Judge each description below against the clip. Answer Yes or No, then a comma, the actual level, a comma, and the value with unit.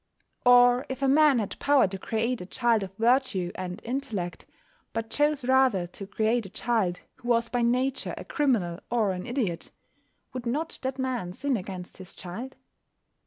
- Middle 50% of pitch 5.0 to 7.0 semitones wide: Yes, average, 5.3 semitones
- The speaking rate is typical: Yes, average, 170 wpm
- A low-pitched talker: No, high, 235 Hz